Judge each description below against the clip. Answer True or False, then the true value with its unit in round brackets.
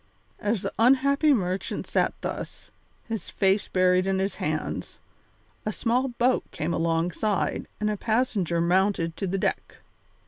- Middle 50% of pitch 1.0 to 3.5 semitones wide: False (4.3 semitones)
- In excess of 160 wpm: False (140 wpm)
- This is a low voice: False (195 Hz)